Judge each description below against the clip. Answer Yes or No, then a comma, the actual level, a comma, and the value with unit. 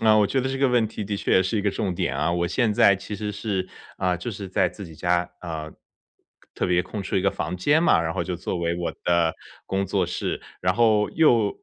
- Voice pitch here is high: No, very low, 95 Hz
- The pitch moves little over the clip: No, average, 3.4 semitones